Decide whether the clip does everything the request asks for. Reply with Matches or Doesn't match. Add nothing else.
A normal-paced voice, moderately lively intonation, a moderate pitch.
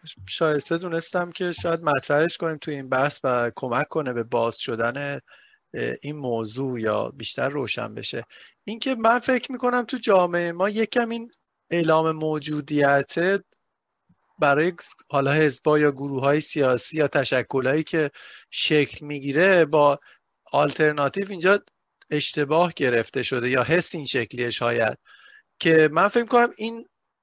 Matches